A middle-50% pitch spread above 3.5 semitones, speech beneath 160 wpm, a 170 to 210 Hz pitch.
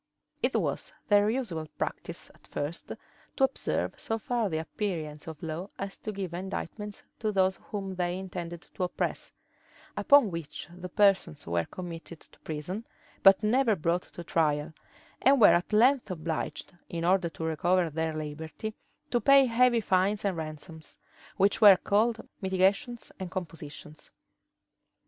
Yes: average, 4.4 semitones; average, 150 wpm; medium, 185 Hz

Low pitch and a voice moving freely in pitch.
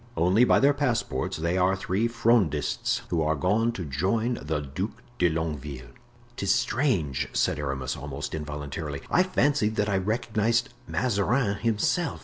Yes: very low, 95 Hz; wide, 7.6 semitones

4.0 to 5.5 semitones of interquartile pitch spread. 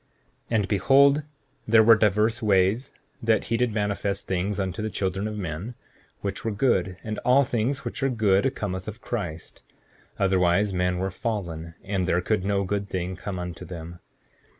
No: average, 3.2 semitones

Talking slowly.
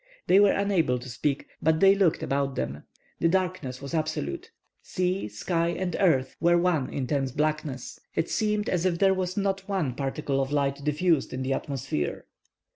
No: average, 175 wpm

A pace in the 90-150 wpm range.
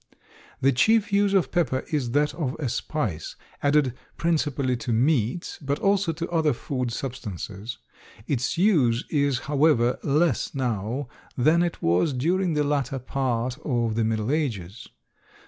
Yes: average, 145 wpm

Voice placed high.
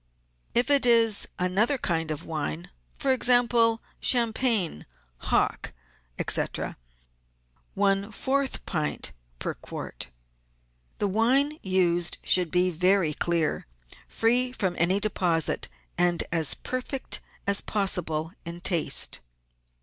Yes: high, 195 Hz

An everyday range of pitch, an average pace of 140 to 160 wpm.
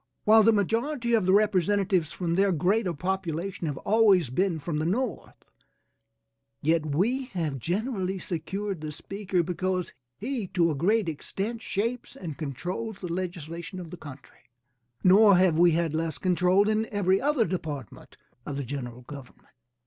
Yes: average, 4.1 semitones; average, 155 wpm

